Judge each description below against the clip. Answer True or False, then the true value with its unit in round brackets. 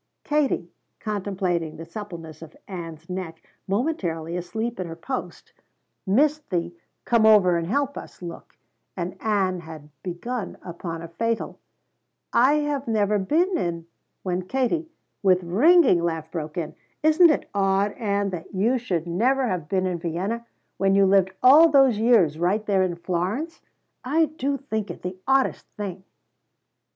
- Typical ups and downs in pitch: False (6.3 semitones)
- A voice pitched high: True (195 Hz)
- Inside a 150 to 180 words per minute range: True (155 wpm)